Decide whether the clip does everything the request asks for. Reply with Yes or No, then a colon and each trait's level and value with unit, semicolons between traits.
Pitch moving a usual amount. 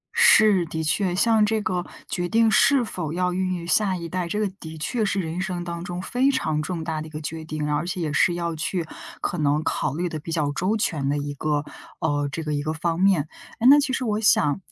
Yes: average, 3.8 semitones